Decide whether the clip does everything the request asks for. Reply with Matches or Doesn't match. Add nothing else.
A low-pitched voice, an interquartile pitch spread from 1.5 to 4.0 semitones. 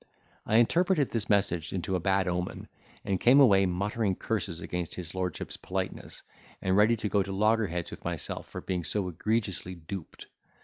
Matches